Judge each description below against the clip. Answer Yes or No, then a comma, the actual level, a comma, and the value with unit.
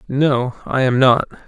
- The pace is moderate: Yes, average, 160 wpm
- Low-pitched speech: Yes, low, 130 Hz